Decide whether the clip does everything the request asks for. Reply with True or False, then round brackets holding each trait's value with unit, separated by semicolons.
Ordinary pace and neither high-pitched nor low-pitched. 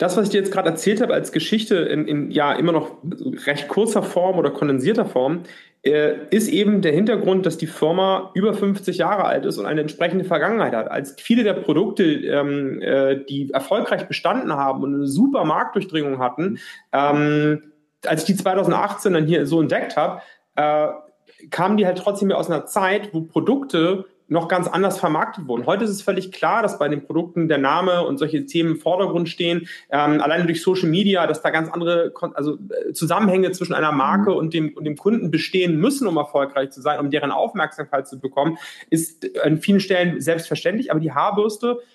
False (195 wpm; 170 Hz)